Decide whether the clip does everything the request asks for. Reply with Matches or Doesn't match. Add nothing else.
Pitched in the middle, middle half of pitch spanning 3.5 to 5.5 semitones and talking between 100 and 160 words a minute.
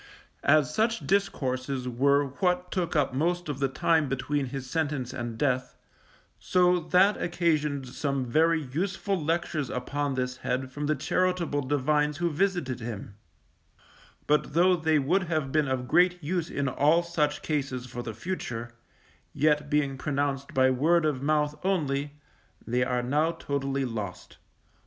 Matches